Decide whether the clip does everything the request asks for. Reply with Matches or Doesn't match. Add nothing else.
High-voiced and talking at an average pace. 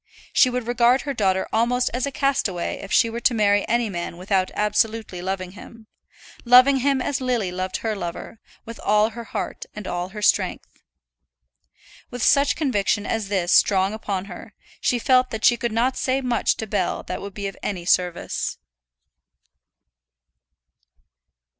Matches